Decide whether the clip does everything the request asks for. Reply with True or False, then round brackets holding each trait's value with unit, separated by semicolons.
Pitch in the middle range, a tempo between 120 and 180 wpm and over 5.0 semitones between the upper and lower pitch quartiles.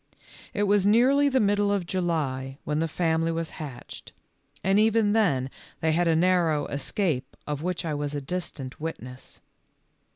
True (165 Hz; 160 wpm; 5.5 semitones)